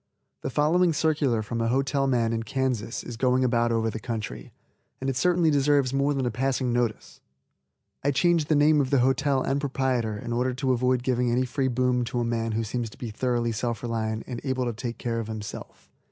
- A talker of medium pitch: No, low, 125 Hz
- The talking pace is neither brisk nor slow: No, fast, 215 wpm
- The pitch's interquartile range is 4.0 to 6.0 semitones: No, average, 2.7 semitones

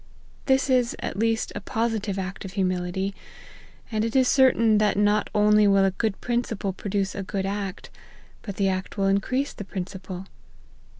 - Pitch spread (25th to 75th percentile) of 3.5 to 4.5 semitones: No, narrow, 2.5 semitones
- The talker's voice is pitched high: Yes, high, 205 Hz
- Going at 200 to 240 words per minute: No, average, 170 wpm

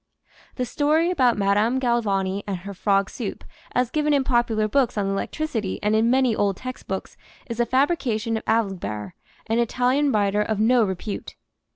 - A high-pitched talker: Yes, high, 225 Hz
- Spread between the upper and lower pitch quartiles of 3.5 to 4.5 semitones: Yes, average, 4.1 semitones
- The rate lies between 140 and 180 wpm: Yes, average, 165 wpm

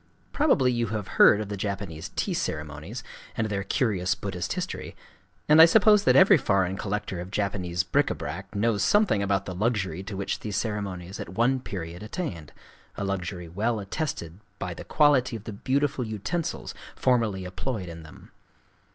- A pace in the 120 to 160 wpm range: No, average, 170 wpm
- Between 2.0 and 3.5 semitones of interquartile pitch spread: No, average, 4.5 semitones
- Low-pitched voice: Yes, low, 100 Hz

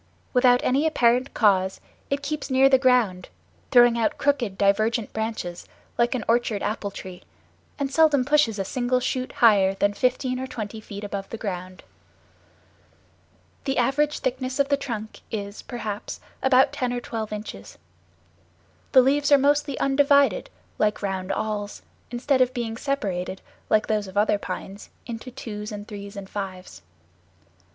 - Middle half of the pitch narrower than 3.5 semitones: No, average, 4.4 semitones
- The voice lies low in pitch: No, high, 230 Hz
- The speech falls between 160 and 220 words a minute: No, average, 150 wpm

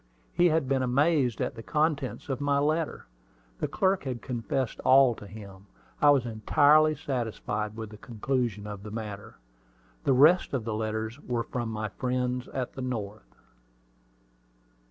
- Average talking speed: Yes, average, 155 wpm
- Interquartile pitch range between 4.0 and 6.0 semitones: Yes, average, 4.4 semitones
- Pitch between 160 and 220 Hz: No, low, 125 Hz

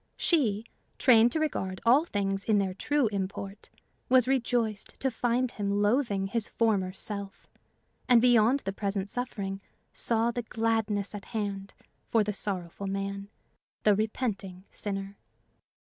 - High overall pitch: Yes, high, 210 Hz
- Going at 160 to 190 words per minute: No, slow, 135 wpm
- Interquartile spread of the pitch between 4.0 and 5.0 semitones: No, average, 3.1 semitones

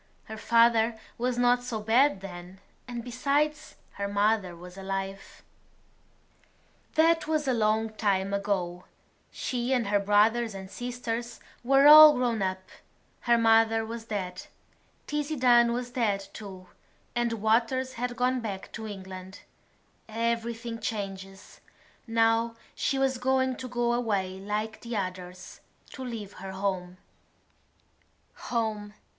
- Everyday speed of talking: No, slow, 130 wpm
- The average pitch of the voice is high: Yes, high, 225 Hz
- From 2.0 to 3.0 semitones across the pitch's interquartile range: No, average, 3.7 semitones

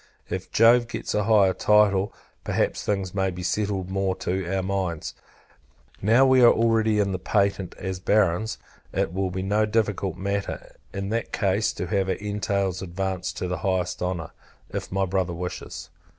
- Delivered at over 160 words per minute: Yes, average, 170 wpm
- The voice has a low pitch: Yes, very low, 95 Hz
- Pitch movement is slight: Yes, narrow, 2.1 semitones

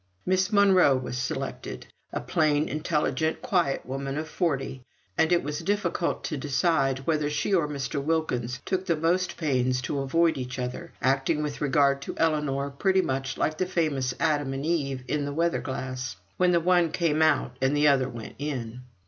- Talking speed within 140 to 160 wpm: No, average, 175 wpm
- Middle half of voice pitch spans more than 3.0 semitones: Yes, average, 3.7 semitones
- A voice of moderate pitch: Yes, medium, 145 Hz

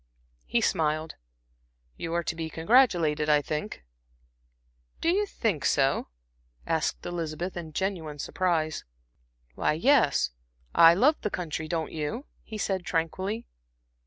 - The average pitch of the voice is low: No, medium, 165 Hz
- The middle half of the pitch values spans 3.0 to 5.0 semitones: Yes, average, 3.7 semitones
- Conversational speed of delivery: No, slow, 125 wpm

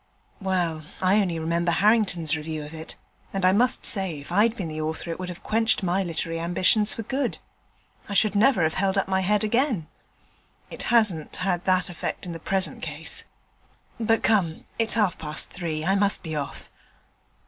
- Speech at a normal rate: Yes, average, 185 wpm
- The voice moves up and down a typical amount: Yes, average, 4.1 semitones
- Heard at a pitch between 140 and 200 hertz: Yes, medium, 185 Hz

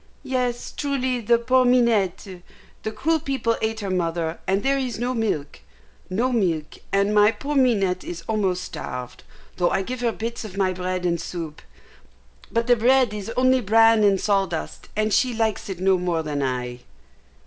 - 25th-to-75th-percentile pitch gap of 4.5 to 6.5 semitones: Yes, average, 5.0 semitones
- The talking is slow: No, average, 175 wpm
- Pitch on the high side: Yes, high, 210 Hz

